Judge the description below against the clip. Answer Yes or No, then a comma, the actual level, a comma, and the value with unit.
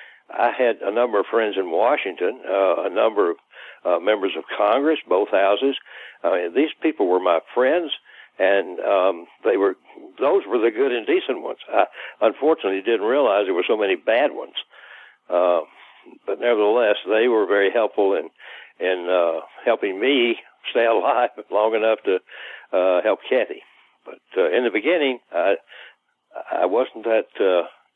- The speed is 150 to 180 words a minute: Yes, average, 165 wpm